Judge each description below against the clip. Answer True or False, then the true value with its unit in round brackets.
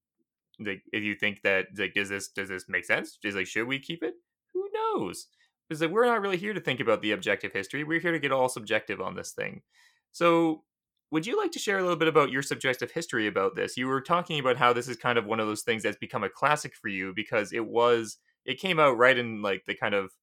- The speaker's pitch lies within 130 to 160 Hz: True (135 Hz)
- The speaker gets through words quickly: True (260 wpm)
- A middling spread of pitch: False (7.4 semitones)